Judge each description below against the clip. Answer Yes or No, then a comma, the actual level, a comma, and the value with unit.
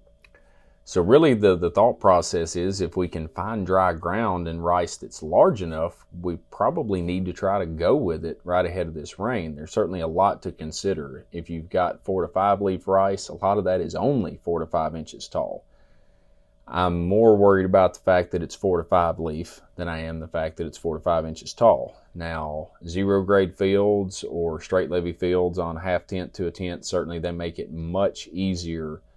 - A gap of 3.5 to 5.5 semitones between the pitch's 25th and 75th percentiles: No, narrow, 2.4 semitones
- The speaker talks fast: Yes, fast, 210 wpm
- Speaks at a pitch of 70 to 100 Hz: Yes, very low, 90 Hz